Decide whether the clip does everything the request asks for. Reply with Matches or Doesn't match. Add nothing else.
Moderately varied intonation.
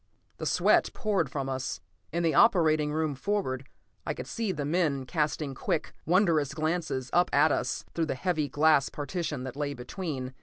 Matches